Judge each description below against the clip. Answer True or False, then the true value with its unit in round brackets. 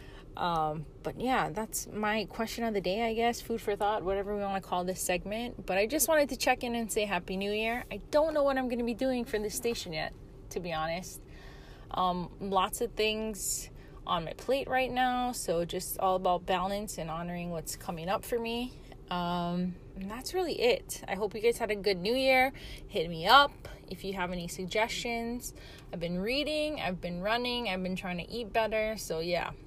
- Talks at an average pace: False (215 wpm)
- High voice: True (215 Hz)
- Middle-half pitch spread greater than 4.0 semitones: True (4.7 semitones)